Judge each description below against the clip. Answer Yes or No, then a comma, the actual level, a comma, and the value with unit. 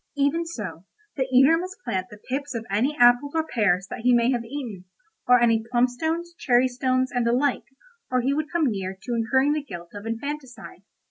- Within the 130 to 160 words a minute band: No, fast, 205 wpm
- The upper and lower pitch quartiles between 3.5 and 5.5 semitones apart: Yes, average, 3.8 semitones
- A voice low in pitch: No, very high, 250 Hz